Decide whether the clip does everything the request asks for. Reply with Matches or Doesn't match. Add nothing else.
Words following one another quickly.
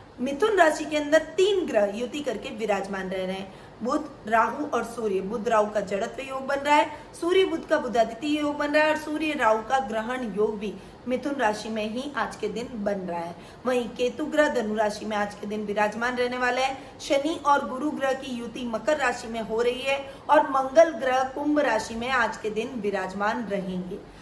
Matches